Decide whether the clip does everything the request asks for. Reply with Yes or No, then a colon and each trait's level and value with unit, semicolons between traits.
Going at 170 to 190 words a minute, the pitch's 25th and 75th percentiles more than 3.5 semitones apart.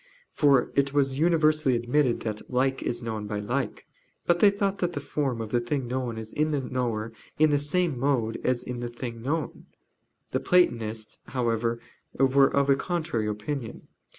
Yes: average, 180 wpm; average, 4.0 semitones